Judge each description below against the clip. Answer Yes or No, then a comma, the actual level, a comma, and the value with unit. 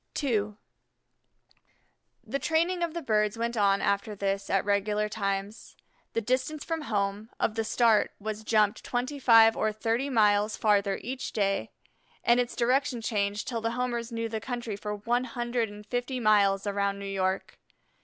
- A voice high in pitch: Yes, high, 220 Hz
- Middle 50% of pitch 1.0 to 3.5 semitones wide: Yes, average, 3.0 semitones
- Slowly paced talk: No, average, 165 wpm